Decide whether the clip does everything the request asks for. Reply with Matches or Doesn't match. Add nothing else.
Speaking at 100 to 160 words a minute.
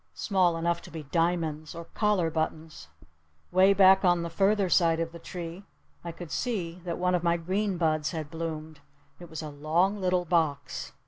Doesn't match